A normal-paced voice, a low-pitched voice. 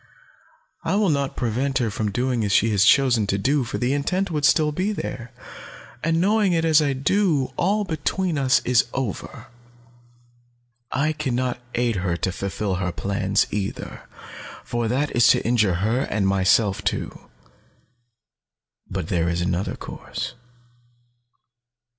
Yes: average, 150 wpm; low, 125 Hz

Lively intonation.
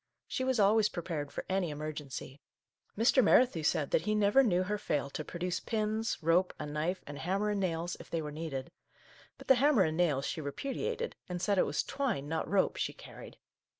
Yes: wide, 5.7 semitones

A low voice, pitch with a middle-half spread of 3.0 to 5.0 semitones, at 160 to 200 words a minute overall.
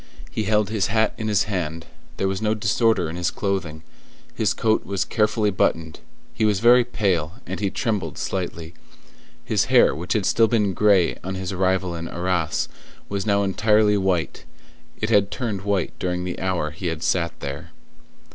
Yes: very low, 95 Hz; average, 3.3 semitones; average, 175 wpm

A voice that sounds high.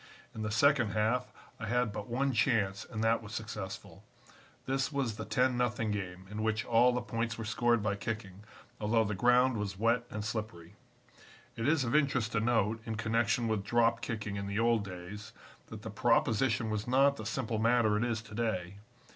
No: low, 110 Hz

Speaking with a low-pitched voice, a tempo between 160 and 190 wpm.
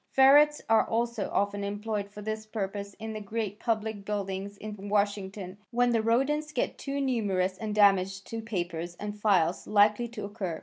No: high, 210 Hz; average, 170 wpm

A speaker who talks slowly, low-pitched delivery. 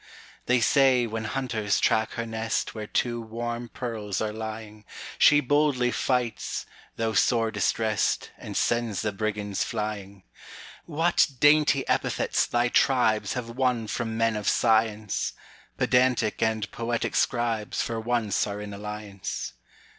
Yes: slow, 110 wpm; low, 115 Hz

